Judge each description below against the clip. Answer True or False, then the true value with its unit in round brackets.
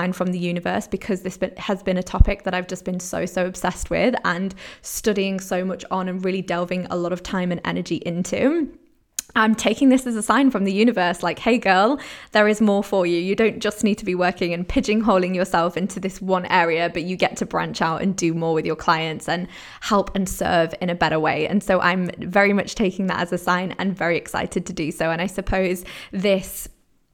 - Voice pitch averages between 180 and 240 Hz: True (185 Hz)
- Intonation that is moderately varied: False (2.3 semitones)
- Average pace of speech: False (230 wpm)